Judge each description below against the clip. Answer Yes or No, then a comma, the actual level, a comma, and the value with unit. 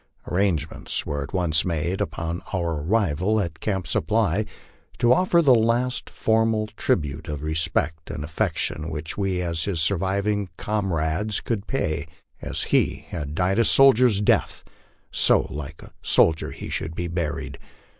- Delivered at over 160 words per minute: No, average, 145 wpm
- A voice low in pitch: Yes, very low, 90 Hz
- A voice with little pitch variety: No, average, 5.1 semitones